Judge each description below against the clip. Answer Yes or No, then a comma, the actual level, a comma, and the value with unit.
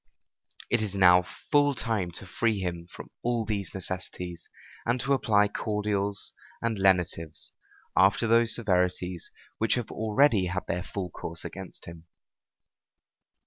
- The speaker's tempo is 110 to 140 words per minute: Yes, slow, 135 wpm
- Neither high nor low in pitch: No, low, 100 Hz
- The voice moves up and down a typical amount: Yes, average, 3.8 semitones